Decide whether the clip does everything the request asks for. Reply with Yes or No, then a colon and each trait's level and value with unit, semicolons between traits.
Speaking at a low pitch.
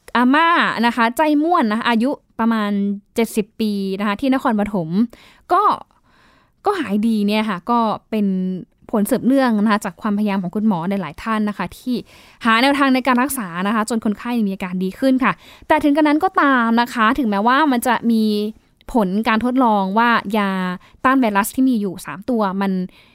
No: high, 225 Hz